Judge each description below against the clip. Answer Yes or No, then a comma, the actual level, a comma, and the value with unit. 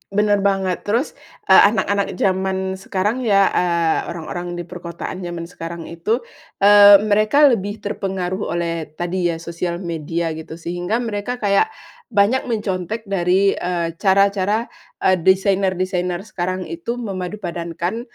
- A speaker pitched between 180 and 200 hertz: Yes, high, 190 Hz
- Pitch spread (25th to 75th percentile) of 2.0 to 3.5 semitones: Yes, average, 3.0 semitones